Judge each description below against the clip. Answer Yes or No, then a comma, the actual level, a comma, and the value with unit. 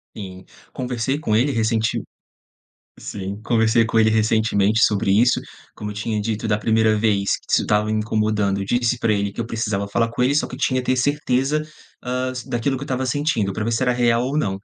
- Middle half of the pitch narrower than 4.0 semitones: Yes, average, 2.9 semitones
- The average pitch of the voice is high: No, low, 110 Hz